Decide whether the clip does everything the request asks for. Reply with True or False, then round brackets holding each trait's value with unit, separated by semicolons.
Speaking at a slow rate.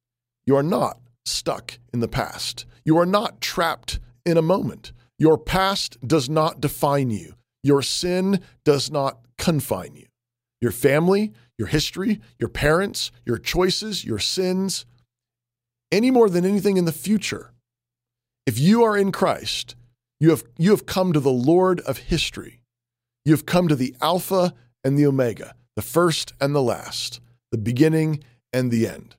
False (160 wpm)